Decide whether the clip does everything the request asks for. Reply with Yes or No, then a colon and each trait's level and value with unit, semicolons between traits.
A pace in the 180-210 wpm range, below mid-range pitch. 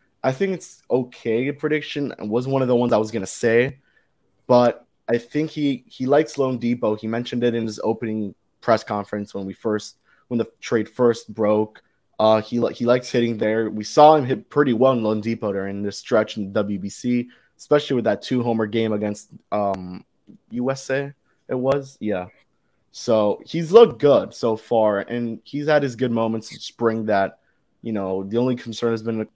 Yes: average, 190 wpm; low, 115 Hz